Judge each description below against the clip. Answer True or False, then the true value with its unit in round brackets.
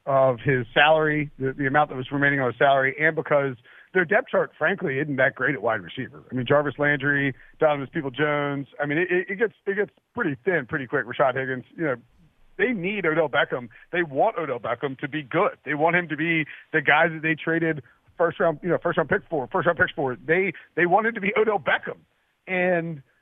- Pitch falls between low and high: True (150 Hz)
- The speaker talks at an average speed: False (225 wpm)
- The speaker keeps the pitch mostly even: False (3.5 semitones)